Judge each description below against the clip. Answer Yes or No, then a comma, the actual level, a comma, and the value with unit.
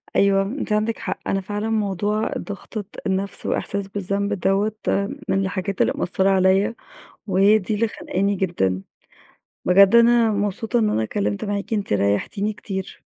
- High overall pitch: Yes, high, 200 Hz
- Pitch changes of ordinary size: No, narrow, 1.8 semitones